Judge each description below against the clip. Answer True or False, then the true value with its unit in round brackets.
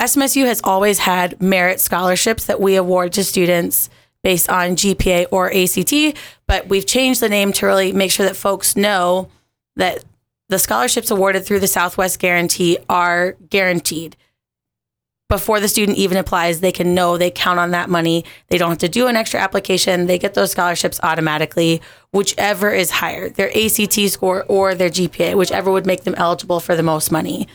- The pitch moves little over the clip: True (2.0 semitones)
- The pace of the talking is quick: False (180 wpm)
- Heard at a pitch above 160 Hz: True (185 Hz)